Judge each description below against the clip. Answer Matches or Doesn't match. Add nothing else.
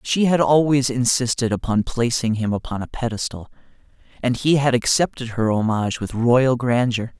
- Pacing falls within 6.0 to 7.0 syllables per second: Doesn't match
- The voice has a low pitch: Matches